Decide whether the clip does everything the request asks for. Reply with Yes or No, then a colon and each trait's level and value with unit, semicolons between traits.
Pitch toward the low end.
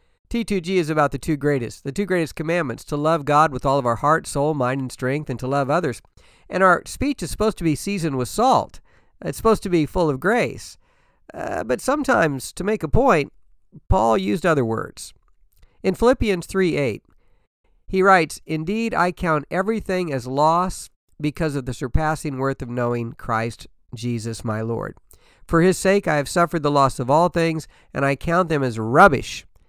No: medium, 155 Hz